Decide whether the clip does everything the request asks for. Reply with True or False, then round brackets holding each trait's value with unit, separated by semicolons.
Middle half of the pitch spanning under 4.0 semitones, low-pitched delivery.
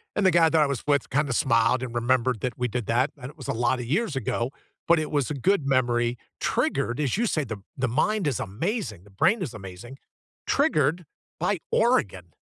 False (4.8 semitones; 130 Hz)